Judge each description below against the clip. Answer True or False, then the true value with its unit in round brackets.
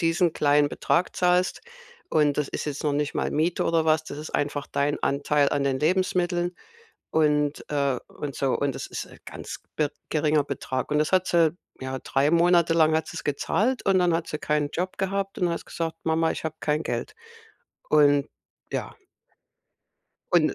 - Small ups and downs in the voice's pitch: False (3.0 semitones)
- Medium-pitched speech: True (155 Hz)